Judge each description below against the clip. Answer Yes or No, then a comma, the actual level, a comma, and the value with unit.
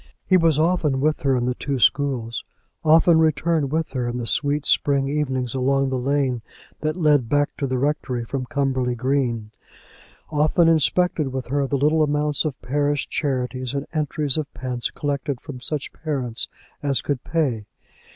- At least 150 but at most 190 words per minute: Yes, average, 170 wpm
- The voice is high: No, medium, 140 Hz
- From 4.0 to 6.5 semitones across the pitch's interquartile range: No, average, 2.9 semitones